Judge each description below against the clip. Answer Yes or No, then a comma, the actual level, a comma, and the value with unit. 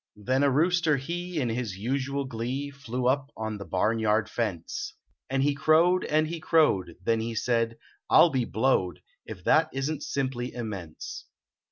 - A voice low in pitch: Yes, low, 130 Hz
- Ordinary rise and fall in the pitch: Yes, average, 4.4 semitones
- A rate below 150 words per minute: No, average, 175 wpm